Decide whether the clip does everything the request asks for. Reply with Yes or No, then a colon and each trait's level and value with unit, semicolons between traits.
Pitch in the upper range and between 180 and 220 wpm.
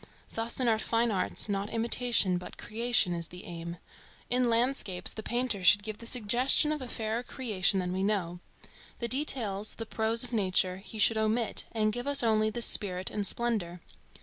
Yes: high, 220 Hz; average, 185 wpm